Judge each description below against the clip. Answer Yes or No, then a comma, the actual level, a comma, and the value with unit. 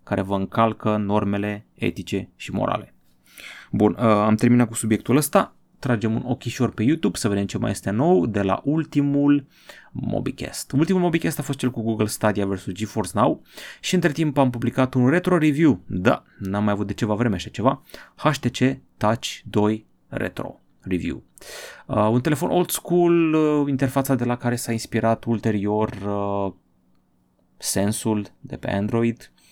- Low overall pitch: Yes, low, 115 Hz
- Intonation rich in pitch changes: No, average, 4.9 semitones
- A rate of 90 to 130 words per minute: No, average, 155 wpm